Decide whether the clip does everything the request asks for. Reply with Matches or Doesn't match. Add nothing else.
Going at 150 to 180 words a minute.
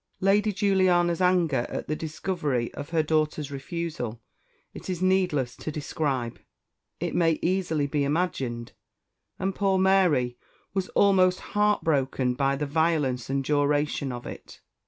Doesn't match